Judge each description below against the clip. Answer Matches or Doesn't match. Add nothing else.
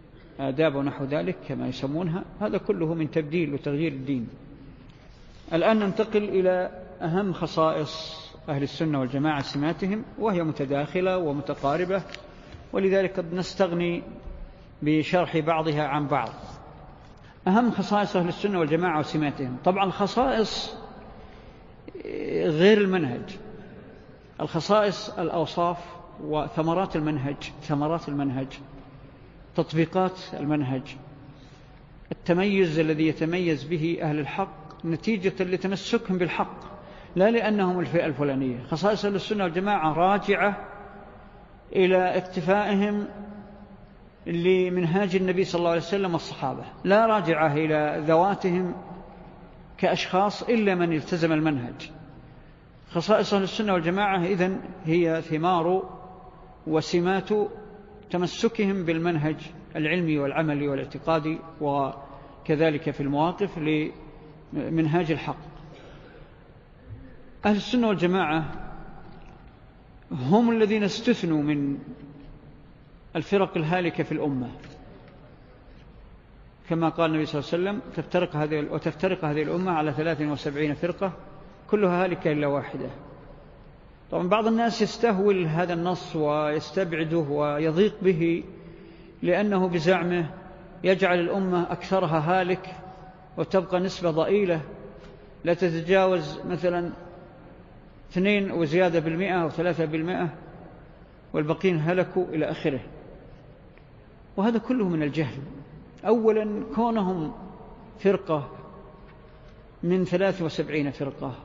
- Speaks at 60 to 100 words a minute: Matches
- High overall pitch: Doesn't match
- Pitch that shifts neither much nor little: Matches